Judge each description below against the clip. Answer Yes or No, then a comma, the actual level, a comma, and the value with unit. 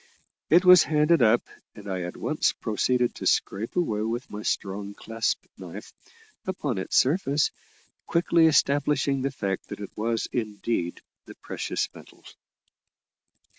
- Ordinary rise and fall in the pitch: No, wide, 6.0 semitones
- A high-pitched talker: No, low, 120 Hz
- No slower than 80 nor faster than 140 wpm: Yes, slow, 135 wpm